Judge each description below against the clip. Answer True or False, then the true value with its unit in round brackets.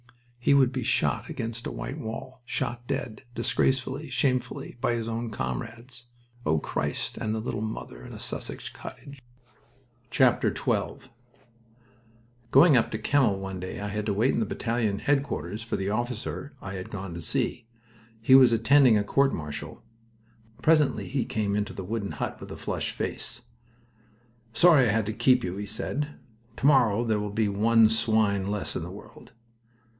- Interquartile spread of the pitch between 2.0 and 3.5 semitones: False (3.9 semitones)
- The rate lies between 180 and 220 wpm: False (165 wpm)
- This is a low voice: True (115 Hz)